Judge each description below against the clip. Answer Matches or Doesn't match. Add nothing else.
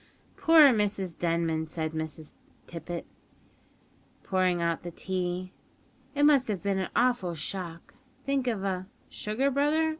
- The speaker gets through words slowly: Matches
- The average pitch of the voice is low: Doesn't match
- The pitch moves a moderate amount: Doesn't match